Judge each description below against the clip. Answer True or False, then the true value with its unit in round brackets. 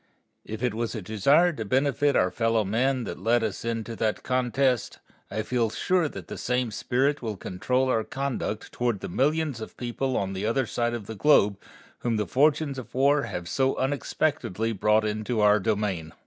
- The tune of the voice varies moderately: True (3.8 semitones)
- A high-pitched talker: False (115 Hz)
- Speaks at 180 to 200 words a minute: True (185 wpm)